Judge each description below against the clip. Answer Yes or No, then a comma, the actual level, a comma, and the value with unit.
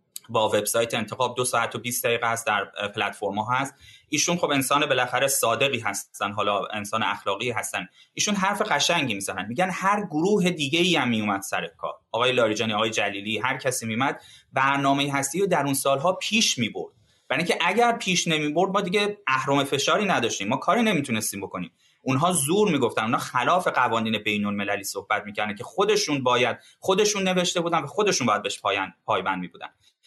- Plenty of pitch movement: Yes, wide, 8.1 semitones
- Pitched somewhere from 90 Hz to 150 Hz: Yes, medium, 140 Hz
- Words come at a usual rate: No, fast, 175 wpm